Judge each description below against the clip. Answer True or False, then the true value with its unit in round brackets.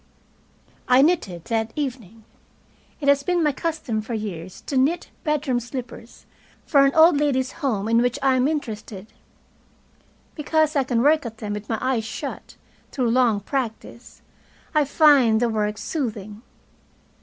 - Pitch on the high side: True (250 Hz)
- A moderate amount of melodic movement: True (4.7 semitones)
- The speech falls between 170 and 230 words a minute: False (150 wpm)